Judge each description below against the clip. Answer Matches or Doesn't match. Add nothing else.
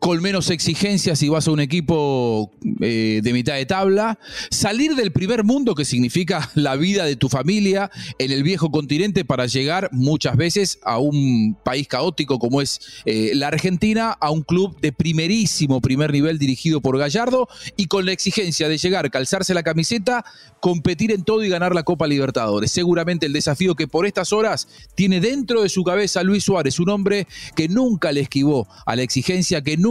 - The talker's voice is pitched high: Doesn't match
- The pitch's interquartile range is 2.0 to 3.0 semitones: Doesn't match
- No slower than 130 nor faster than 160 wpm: Doesn't match